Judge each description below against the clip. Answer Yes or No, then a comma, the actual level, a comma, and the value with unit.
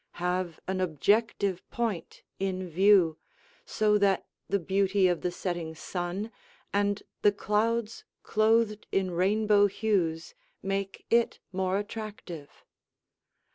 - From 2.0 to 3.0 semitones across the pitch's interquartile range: Yes, average, 2.7 semitones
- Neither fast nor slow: No, slow, 110 wpm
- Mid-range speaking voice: No, high, 195 Hz